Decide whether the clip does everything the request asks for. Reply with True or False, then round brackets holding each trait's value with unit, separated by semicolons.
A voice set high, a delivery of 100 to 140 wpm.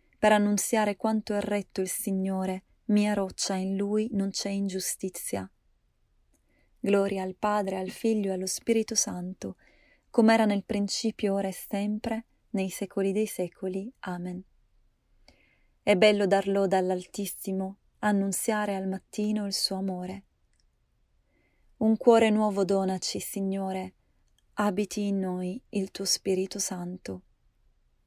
True (195 Hz; 125 wpm)